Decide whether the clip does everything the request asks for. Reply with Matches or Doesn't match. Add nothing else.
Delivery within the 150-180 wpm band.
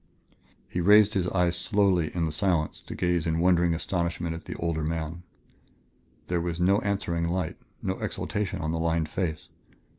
Matches